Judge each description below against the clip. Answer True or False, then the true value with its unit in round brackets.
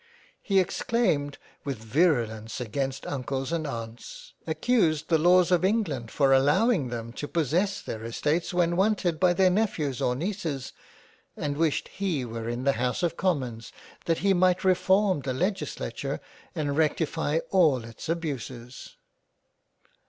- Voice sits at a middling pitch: True (155 Hz)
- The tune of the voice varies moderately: False (6.0 semitones)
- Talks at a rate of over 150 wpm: False (145 wpm)